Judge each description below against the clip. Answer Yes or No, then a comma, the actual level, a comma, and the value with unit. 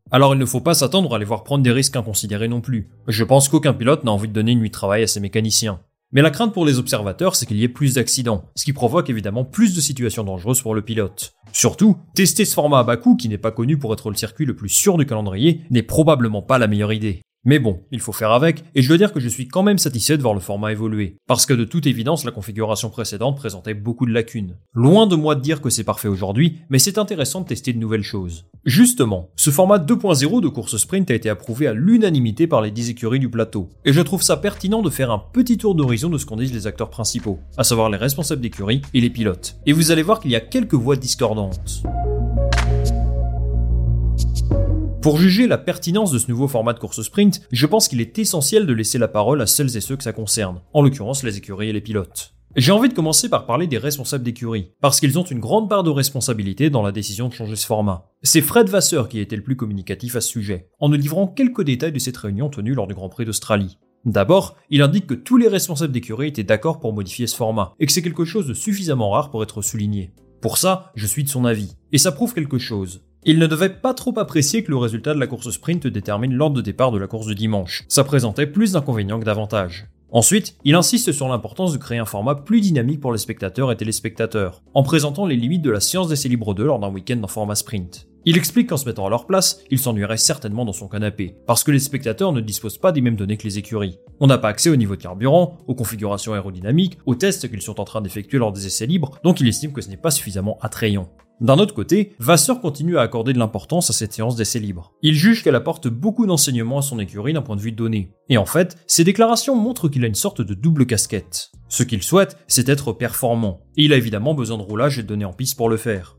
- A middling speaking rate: No, fast, 250 wpm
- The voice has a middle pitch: No, low, 120 Hz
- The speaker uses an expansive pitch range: Yes, wide, 6.2 semitones